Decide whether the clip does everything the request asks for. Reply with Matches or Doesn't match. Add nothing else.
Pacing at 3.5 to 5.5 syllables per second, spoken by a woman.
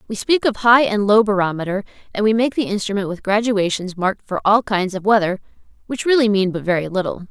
Doesn't match